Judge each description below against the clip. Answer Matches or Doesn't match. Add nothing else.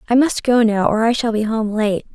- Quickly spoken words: Matches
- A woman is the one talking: Matches